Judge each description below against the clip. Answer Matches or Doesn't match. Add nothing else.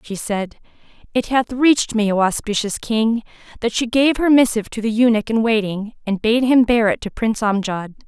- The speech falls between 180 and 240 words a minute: Matches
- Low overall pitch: Doesn't match